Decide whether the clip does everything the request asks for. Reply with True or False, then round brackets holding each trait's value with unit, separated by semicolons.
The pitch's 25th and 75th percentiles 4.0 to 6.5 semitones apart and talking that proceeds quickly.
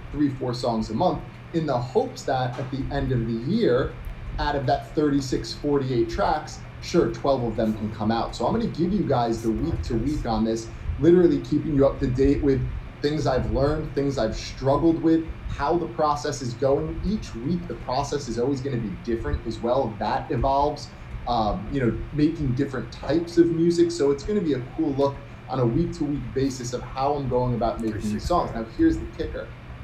True (4.3 semitones; 210 wpm)